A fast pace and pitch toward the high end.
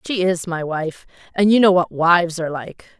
No: fast, 220 wpm; medium, 175 Hz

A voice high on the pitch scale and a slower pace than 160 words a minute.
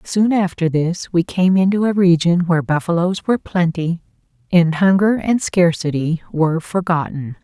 No: medium, 175 Hz; average, 145 wpm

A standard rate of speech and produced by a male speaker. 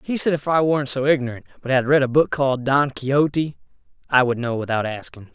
No: fast, 225 wpm; male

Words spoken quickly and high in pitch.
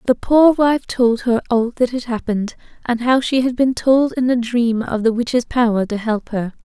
Yes: fast, 225 wpm; high, 240 Hz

